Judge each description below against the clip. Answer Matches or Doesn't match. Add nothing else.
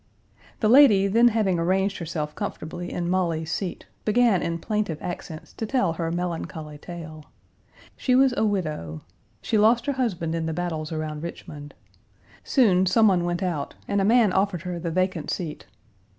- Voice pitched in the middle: Matches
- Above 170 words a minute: Doesn't match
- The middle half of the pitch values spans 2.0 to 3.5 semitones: Doesn't match